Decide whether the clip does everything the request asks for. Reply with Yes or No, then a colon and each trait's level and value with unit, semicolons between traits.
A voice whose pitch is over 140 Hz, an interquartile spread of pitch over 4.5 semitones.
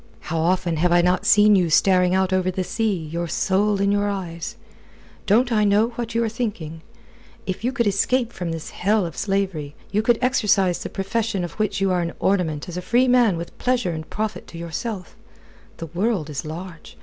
No: high, 190 Hz; average, 3.9 semitones